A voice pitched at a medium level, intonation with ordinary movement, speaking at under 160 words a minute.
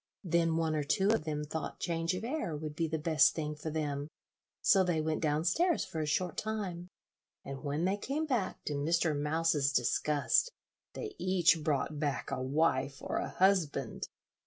No: medium, 160 Hz; average, 3.3 semitones; average, 185 wpm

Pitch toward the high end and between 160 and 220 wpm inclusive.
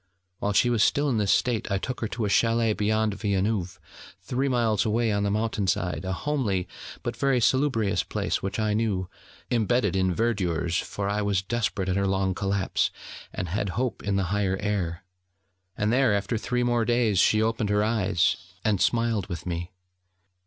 No: low, 105 Hz; average, 185 wpm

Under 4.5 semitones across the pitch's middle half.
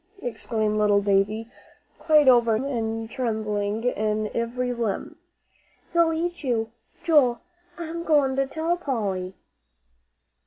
No: average, 4.8 semitones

